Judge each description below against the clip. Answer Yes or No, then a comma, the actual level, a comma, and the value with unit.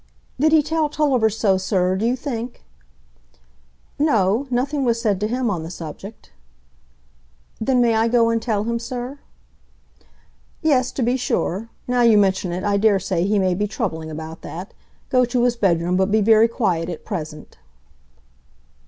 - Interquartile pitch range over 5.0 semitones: No, average, 4.5 semitones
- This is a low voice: No, high, 220 Hz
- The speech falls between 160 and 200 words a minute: Yes, average, 170 wpm